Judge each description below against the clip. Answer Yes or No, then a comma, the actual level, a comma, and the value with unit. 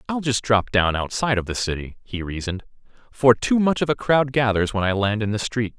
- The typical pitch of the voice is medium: No, low, 115 Hz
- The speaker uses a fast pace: Yes, fast, 240 wpm